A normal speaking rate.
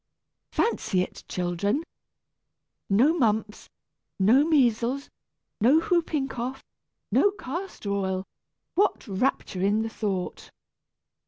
No: slow, 95 wpm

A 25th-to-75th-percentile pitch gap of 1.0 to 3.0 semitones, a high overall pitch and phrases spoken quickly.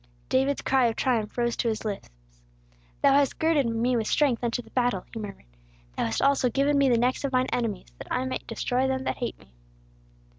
Yes: average, 2.7 semitones; very high, 250 Hz; fast, 215 wpm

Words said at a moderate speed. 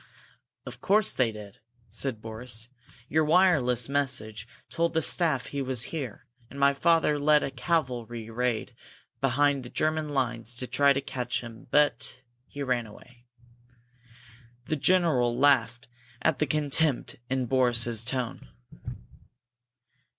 No: slow, 130 wpm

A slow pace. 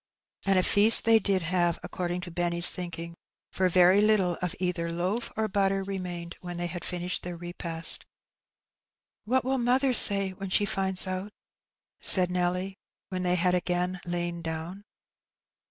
No: average, 170 wpm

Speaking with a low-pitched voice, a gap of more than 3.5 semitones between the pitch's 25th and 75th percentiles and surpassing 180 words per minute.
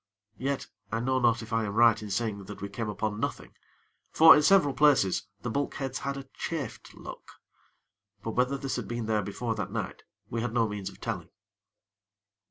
Yes: low, 115 Hz; average, 4.0 semitones; average, 190 wpm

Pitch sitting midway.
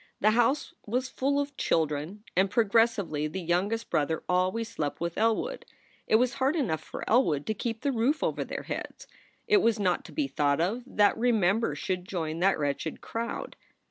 No: high, 210 Hz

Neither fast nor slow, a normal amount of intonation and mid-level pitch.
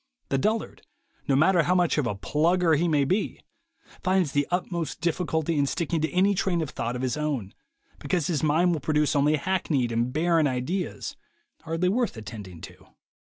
Yes: average, 180 wpm; average, 4.2 semitones; medium, 155 Hz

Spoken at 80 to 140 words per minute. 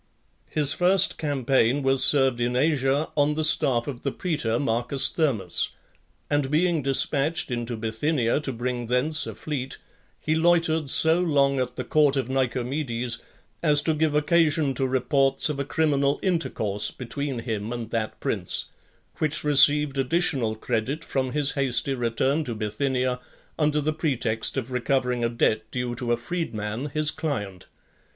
No: average, 160 wpm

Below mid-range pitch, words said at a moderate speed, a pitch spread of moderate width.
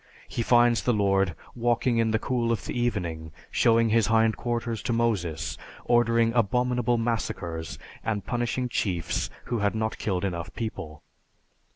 Yes: low, 115 Hz; average, 150 wpm; average, 3.5 semitones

